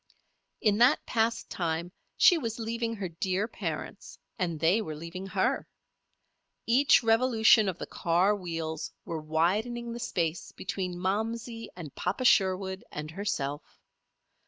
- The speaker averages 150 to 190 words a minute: No, slow, 135 wpm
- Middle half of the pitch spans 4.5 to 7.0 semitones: Yes, average, 5.2 semitones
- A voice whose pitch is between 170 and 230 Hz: Yes, high, 190 Hz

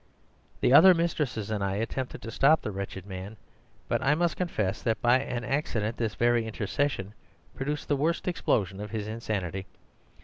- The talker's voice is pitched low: Yes, low, 115 Hz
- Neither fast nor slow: Yes, average, 170 wpm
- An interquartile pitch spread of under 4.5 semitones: No, wide, 5.6 semitones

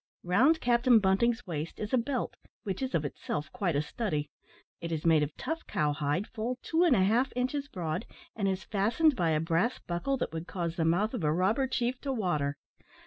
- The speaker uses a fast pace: Yes, fast, 210 wpm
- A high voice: Yes, high, 195 Hz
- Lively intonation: Yes, wide, 7.3 semitones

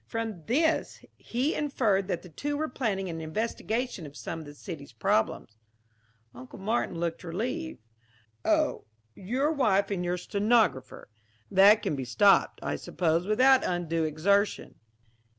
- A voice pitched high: Yes, high, 195 Hz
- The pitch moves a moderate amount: No, wide, 6.2 semitones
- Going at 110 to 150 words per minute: Yes, average, 140 wpm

